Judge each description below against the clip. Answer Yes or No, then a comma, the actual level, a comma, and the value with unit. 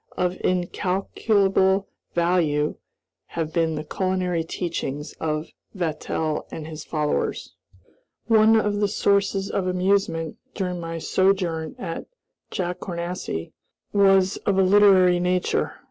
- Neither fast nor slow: No, slow, 110 wpm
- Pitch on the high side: No, medium, 180 Hz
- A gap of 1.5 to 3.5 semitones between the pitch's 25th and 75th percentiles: Yes, average, 2.9 semitones